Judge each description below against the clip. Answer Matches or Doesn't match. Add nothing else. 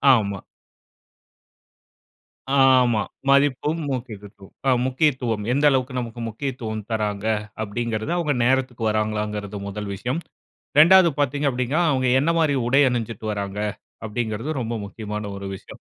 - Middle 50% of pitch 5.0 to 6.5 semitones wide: Doesn't match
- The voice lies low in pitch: Matches